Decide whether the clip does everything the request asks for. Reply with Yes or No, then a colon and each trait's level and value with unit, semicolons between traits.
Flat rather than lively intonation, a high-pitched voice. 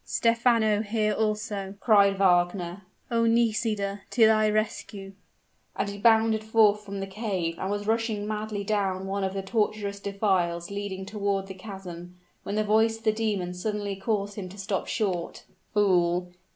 Yes: narrow, 2.0 semitones; high, 205 Hz